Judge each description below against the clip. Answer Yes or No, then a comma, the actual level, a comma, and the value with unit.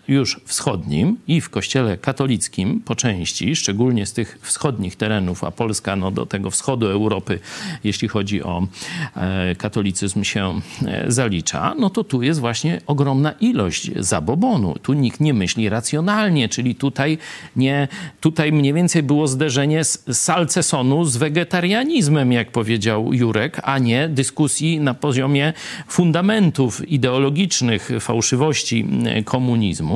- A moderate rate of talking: Yes, average, 130 wpm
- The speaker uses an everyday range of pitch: No, wide, 6.1 semitones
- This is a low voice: Yes, low, 130 Hz